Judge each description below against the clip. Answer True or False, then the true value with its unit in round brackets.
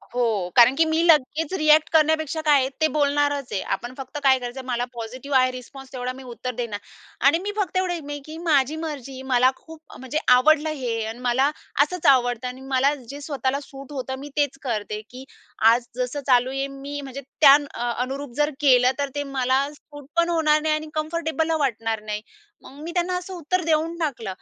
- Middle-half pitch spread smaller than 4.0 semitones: True (3.5 semitones)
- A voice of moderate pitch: False (275 Hz)